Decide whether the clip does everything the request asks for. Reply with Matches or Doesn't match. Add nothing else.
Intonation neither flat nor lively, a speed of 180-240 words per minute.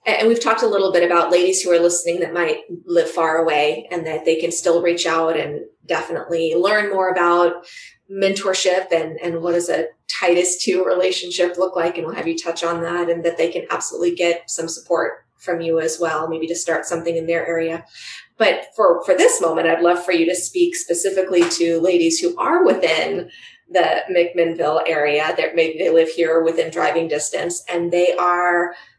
Doesn't match